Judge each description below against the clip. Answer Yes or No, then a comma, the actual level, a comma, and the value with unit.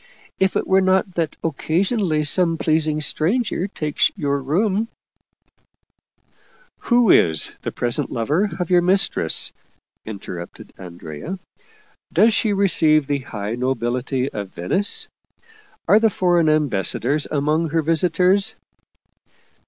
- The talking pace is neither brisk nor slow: No, slow, 120 wpm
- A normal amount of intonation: No, wide, 6.1 semitones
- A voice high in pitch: No, medium, 160 Hz